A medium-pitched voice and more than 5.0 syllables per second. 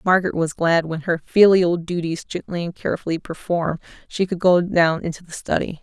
Yes: medium, 170 Hz; 5.5 syllables/s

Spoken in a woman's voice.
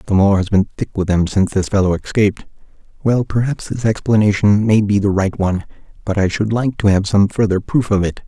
No: male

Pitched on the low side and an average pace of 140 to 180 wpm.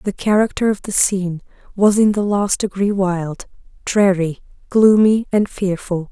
No: high, 195 Hz; average, 145 wpm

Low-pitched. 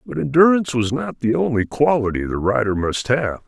Yes: low, 130 Hz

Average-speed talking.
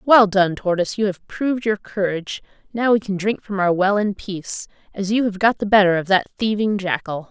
No: fast, 220 wpm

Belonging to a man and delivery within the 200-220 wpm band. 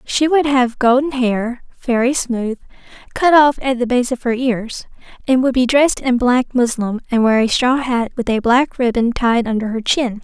No: female; fast, 205 wpm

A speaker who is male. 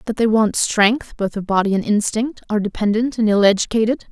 No: female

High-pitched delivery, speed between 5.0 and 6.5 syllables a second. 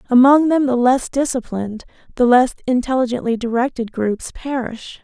Yes: very high, 250 Hz; 5.1 syllables/s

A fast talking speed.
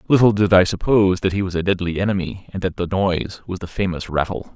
Yes: fast, 235 wpm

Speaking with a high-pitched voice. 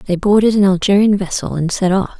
Yes: high, 195 Hz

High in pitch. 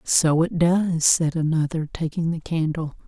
No: medium, 160 Hz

